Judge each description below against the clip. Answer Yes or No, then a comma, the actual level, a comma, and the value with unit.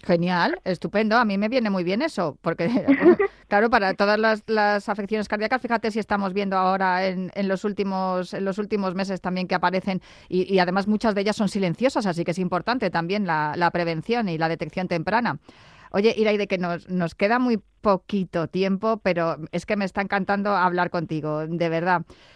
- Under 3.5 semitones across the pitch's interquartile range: Yes, average, 3.0 semitones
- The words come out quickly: Yes, fast, 195 wpm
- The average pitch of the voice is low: No, high, 195 Hz